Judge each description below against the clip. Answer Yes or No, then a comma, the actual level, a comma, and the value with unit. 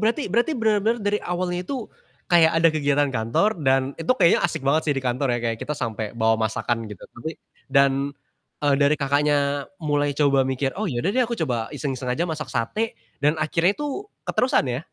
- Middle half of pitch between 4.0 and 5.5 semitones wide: Yes, average, 5.0 semitones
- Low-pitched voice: No, medium, 145 Hz